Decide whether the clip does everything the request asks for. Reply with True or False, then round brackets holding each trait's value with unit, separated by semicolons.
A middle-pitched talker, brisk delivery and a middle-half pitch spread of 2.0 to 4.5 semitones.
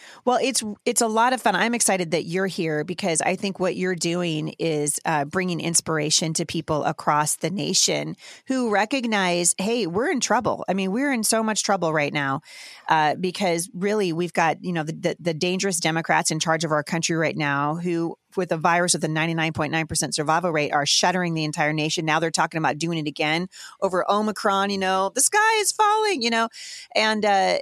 True (175 Hz; 215 wpm; 4.0 semitones)